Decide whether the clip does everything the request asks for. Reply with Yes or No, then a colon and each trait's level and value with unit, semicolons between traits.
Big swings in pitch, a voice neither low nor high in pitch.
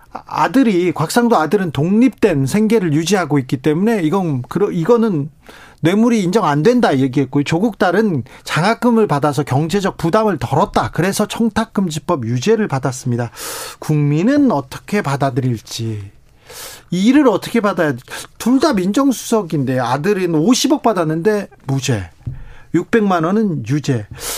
Yes: wide, 7.6 semitones; medium, 175 Hz